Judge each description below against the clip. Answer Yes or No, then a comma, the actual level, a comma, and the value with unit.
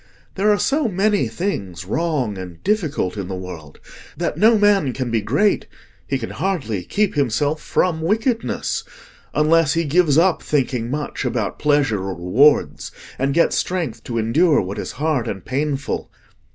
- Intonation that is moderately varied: No, wide, 8.0 semitones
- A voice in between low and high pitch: Yes, medium, 145 Hz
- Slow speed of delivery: No, average, 150 wpm